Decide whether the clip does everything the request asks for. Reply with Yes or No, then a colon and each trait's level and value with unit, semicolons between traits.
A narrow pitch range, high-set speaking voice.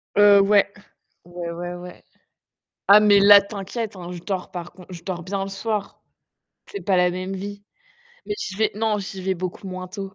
Yes: narrow, 2.1 semitones; high, 195 Hz